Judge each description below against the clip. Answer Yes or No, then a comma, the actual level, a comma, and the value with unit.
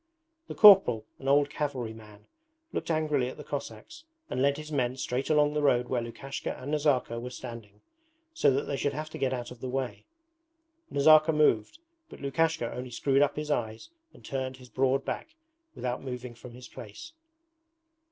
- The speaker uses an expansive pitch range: No, average, 3.2 semitones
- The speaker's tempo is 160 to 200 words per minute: Yes, average, 180 wpm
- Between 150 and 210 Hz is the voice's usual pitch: No, low, 135 Hz